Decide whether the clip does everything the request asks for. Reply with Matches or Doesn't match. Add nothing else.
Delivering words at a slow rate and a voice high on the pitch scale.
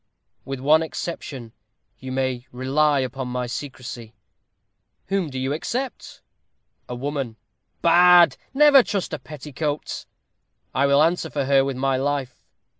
Doesn't match